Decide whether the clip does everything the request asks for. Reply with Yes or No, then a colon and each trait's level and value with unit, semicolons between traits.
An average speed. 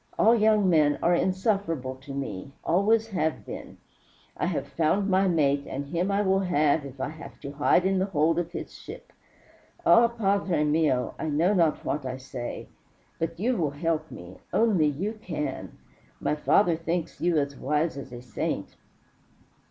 Yes: average, 175 wpm